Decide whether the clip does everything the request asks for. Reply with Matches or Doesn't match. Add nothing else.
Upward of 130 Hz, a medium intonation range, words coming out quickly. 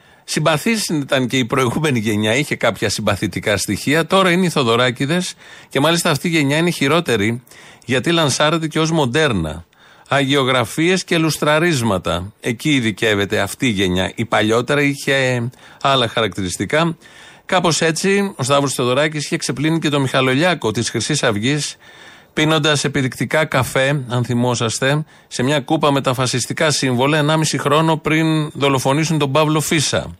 Doesn't match